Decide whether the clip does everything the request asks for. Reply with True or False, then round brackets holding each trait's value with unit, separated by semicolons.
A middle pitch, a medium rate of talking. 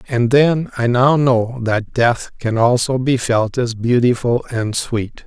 False (120 Hz; 170 wpm)